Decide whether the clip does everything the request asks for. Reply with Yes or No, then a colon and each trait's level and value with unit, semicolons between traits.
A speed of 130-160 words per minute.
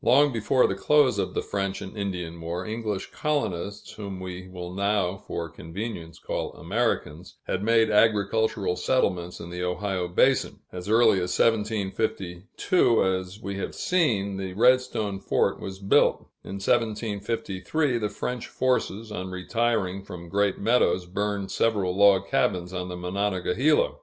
Yes: average, 140 wpm